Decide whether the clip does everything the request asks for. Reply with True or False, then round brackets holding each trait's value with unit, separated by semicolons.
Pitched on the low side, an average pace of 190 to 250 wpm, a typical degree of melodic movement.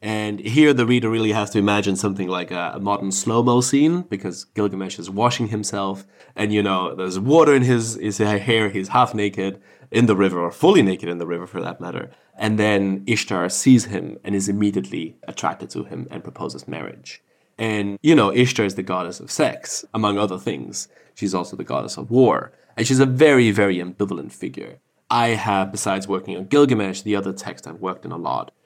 True (105 Hz; 205 wpm; 3.0 semitones)